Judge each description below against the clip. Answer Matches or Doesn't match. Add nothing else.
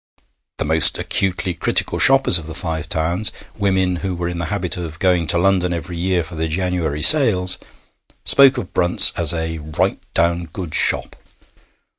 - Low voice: Matches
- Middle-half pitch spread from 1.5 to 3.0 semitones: Matches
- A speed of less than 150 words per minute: Doesn't match